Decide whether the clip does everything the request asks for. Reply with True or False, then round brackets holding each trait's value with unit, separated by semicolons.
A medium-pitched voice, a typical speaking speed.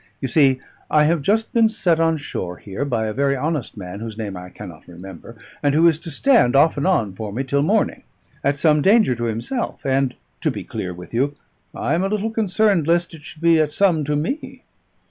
False (145 Hz; 220 wpm)